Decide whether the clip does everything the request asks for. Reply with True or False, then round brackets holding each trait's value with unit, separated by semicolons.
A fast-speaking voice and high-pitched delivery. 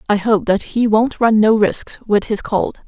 True (230 wpm; 215 Hz)